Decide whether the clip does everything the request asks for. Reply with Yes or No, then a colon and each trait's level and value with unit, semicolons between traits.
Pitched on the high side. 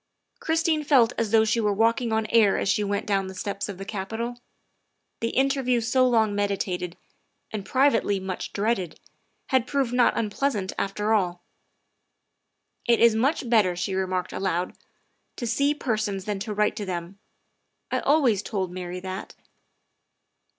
Yes: high, 215 Hz